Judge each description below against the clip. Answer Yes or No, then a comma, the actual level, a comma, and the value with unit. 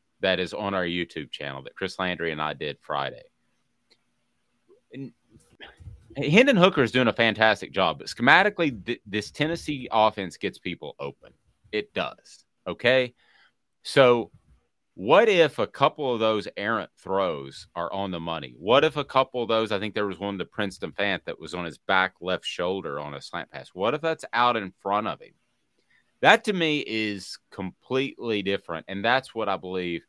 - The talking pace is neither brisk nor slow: Yes, average, 180 wpm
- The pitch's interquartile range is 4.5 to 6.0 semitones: Yes, wide, 5.5 semitones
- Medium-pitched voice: No, low, 105 Hz